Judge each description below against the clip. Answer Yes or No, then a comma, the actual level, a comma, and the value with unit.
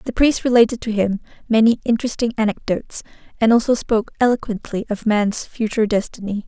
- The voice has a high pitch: Yes, high, 225 Hz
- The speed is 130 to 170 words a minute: Yes, average, 150 wpm